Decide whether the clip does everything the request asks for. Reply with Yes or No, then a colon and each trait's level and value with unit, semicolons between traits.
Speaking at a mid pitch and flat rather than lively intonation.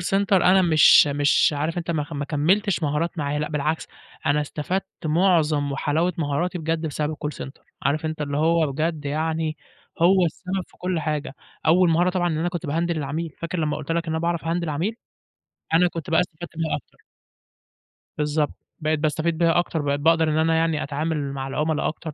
Yes: medium, 160 Hz; narrow, 2.3 semitones